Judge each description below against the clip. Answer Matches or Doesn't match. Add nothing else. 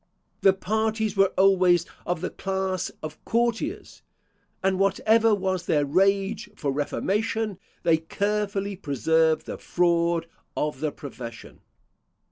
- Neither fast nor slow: Doesn't match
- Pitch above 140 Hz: Matches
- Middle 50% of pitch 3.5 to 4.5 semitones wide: Matches